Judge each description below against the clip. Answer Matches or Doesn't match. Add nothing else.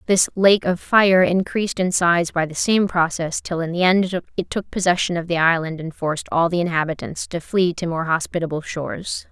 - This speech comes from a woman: Matches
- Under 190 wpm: Doesn't match